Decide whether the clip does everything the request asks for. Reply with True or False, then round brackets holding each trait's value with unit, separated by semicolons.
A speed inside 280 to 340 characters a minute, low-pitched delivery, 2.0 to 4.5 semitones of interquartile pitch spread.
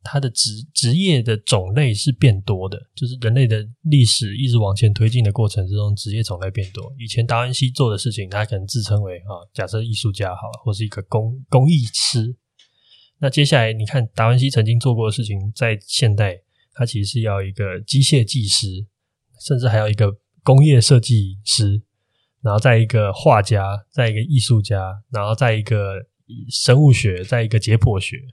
True (285 characters per minute; 115 Hz; 3.3 semitones)